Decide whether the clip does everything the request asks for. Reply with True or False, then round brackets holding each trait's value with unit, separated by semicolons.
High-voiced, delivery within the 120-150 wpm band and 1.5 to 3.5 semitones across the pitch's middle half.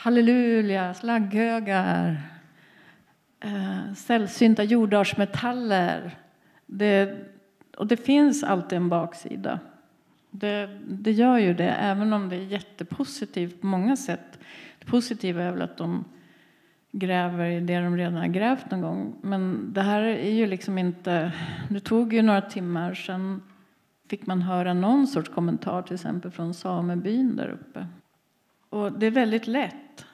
False (200 Hz; 135 wpm; 3.9 semitones)